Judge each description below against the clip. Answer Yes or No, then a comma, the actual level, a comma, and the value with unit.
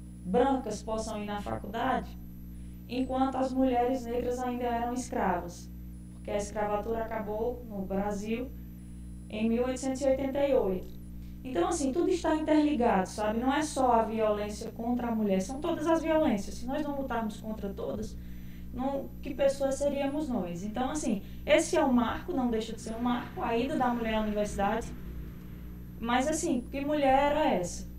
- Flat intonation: No, average, 5.2 semitones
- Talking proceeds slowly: No, average, 160 wpm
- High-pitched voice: Yes, high, 230 Hz